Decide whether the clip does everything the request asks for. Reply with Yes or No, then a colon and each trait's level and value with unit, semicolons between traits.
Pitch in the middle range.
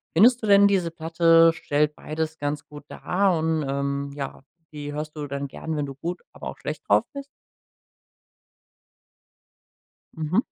Yes: medium, 155 Hz